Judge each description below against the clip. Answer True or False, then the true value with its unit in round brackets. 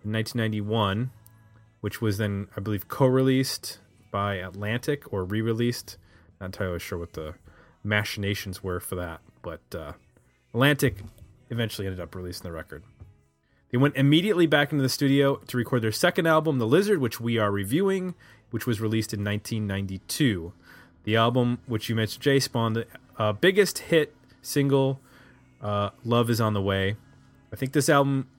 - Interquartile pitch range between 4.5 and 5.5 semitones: True (4.8 semitones)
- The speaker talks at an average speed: True (165 wpm)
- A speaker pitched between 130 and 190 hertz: False (110 Hz)